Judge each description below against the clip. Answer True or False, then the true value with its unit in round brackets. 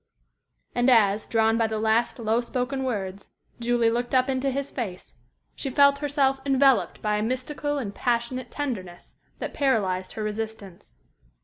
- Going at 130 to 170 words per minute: True (150 wpm)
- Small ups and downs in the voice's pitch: False (3.8 semitones)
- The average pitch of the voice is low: False (235 Hz)